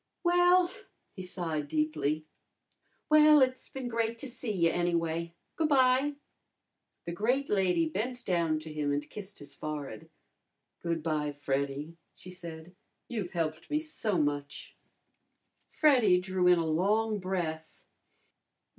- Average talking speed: No, slow, 130 wpm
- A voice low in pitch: No, medium, 180 Hz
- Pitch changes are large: Yes, wide, 7.3 semitones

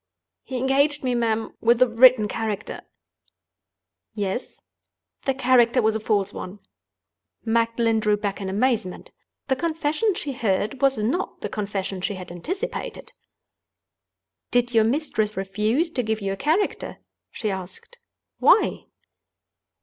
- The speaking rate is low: Yes, slow, 130 wpm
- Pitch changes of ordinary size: Yes, average, 4.2 semitones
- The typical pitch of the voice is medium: No, high, 230 Hz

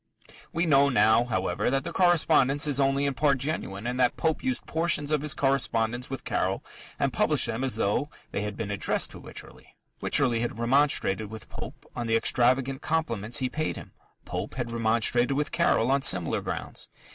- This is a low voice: Yes, low, 130 Hz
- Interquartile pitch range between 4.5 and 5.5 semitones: No, average, 4.1 semitones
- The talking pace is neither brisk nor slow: Yes, average, 185 wpm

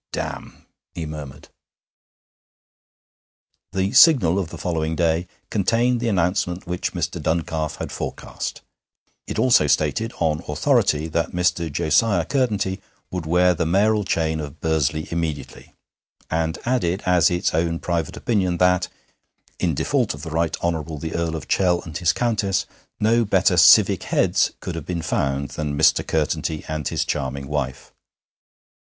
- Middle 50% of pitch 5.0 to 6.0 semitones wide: No, average, 3.1 semitones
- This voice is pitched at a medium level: No, very low, 85 Hz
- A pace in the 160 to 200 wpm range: No, average, 145 wpm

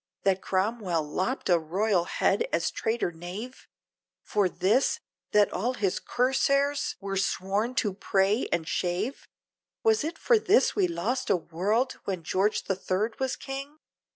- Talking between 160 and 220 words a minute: No, average, 150 wpm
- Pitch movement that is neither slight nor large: No, wide, 5.7 semitones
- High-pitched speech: Yes, high, 210 Hz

